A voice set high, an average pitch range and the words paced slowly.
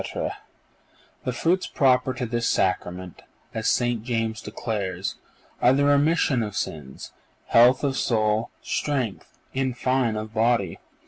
No: low, 120 Hz; average, 3.3 semitones; slow, 125 wpm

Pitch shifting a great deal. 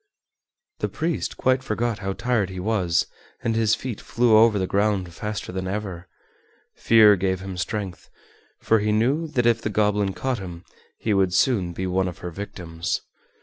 No: average, 3.3 semitones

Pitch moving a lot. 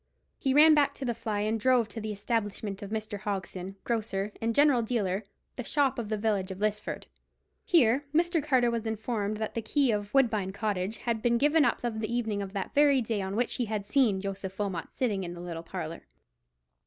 No: average, 3.3 semitones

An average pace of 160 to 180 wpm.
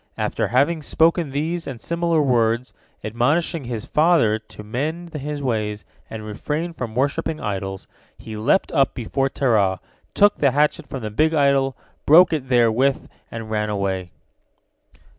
No: average, 145 wpm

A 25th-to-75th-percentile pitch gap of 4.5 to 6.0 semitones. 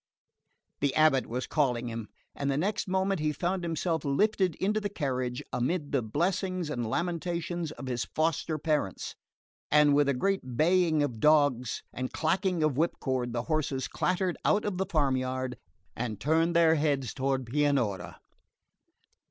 Yes: average, 4.9 semitones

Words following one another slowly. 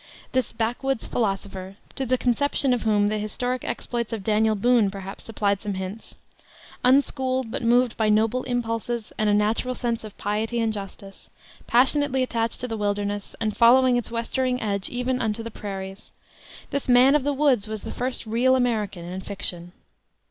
No: average, 170 wpm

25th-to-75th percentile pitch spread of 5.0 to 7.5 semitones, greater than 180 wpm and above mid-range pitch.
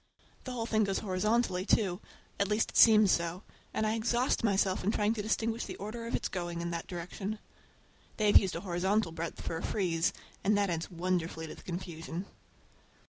No: average, 3.9 semitones; average, 195 wpm; high, 195 Hz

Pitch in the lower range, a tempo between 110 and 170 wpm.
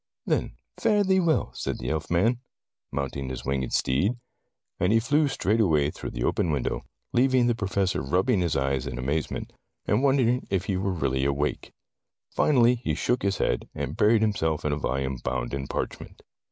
No: very low, 90 Hz; average, 180 wpm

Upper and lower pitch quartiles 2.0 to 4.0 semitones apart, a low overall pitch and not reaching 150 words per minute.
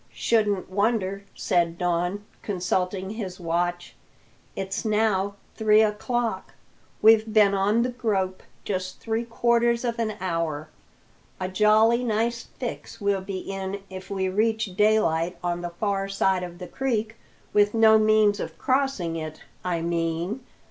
No: average, 3.2 semitones; high, 200 Hz; average, 140 wpm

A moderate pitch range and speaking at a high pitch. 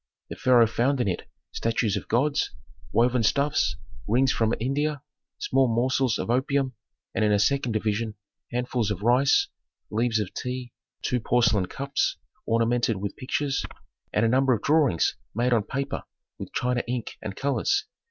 No: average, 3.2 semitones; low, 120 Hz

